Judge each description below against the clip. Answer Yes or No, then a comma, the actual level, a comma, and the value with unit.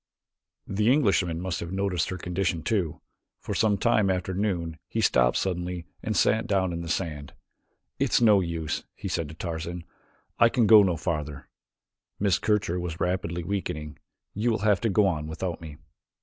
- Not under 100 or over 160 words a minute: No, average, 175 wpm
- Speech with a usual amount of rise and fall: Yes, average, 3.4 semitones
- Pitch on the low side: Yes, very low, 90 Hz